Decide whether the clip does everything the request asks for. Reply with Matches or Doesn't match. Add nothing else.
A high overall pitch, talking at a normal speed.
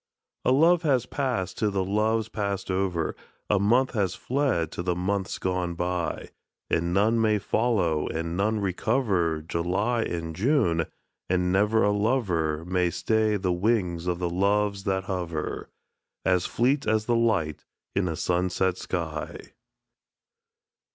Doesn't match